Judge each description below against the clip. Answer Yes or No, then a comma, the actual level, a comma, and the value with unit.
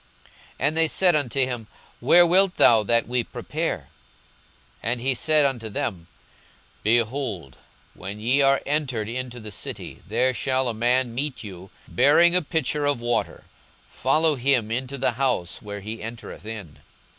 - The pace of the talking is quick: No, average, 160 wpm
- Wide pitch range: No, average, 4.0 semitones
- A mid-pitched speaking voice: No, low, 125 Hz